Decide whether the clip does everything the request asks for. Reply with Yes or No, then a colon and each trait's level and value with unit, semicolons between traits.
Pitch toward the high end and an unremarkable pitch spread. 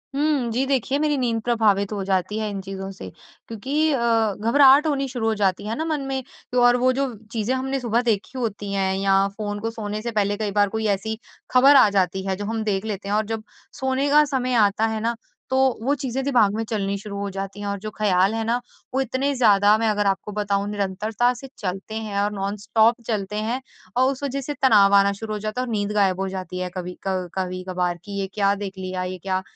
Yes: high, 215 Hz; average, 3.8 semitones